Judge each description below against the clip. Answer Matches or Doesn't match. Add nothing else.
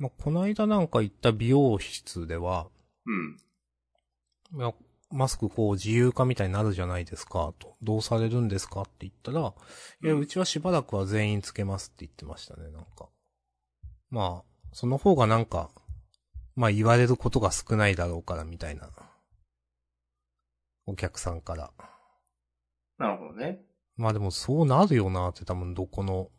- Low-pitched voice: Matches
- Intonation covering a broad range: Matches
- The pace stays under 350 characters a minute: Matches